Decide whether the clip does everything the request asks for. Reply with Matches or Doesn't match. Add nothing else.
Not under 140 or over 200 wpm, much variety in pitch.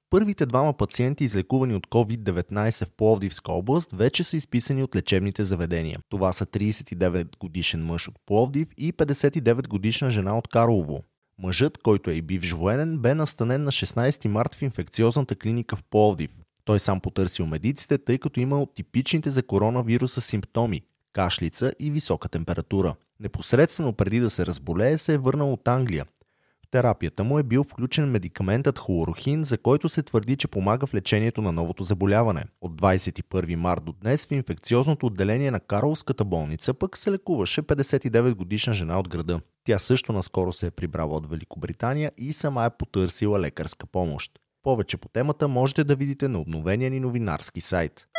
Matches